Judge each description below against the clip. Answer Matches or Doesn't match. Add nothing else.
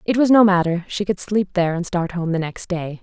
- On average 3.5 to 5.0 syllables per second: Doesn't match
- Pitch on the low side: Doesn't match